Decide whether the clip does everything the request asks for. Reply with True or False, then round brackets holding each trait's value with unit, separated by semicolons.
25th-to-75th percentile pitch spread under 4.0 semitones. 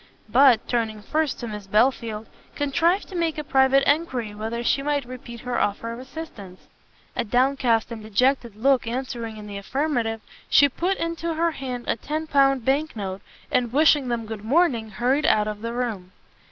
False (4.3 semitones)